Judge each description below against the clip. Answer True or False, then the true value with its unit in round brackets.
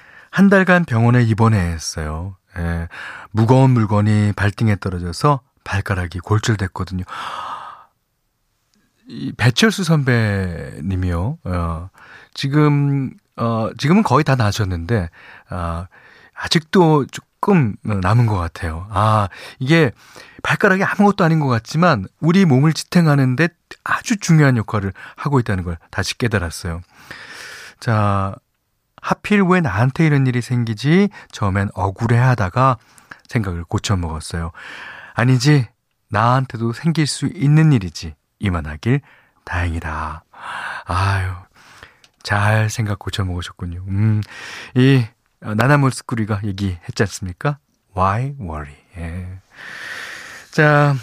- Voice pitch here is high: False (110 Hz)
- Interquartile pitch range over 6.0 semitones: True (6.7 semitones)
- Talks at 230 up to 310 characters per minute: True (250 characters per minute)